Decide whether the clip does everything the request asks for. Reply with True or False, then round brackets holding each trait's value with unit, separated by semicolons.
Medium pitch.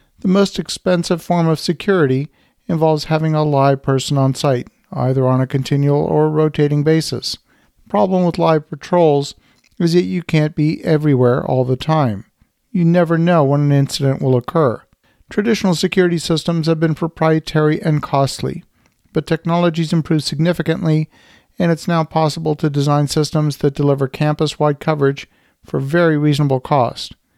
True (155 Hz)